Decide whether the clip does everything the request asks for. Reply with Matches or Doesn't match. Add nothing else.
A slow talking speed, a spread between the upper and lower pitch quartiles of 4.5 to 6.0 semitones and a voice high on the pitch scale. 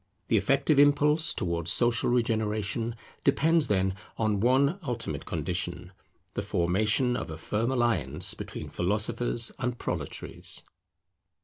Doesn't match